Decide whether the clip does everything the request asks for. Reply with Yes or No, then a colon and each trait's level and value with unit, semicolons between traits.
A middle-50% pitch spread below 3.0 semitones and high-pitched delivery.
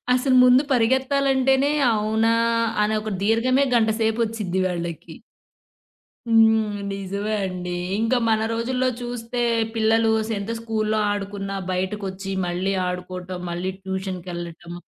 No: average, 3.3 semitones; high, 215 Hz